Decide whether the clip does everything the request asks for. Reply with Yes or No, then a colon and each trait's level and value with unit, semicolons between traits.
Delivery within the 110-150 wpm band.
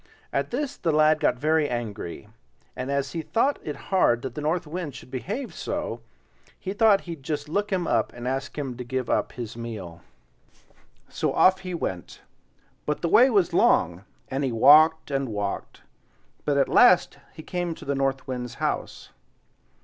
No: average, 180 wpm